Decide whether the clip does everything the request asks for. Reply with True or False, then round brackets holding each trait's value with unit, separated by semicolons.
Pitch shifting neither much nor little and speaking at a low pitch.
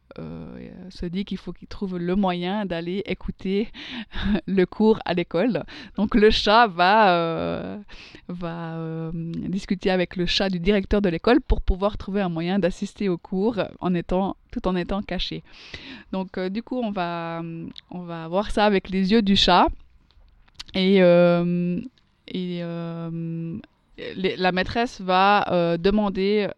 False (3.0 semitones; 185 Hz)